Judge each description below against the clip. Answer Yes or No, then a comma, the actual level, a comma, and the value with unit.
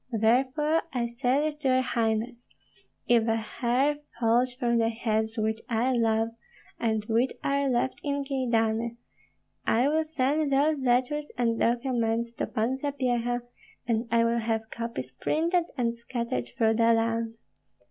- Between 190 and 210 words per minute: No, average, 145 wpm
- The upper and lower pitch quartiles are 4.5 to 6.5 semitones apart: No, narrow, 2.6 semitones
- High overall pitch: Yes, high, 235 Hz